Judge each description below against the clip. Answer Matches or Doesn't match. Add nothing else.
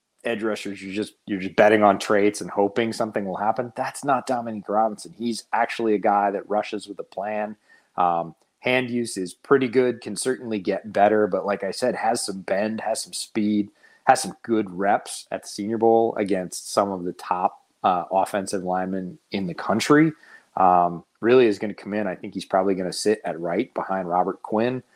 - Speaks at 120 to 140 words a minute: Doesn't match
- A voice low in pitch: Matches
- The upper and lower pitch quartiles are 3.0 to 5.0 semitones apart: Doesn't match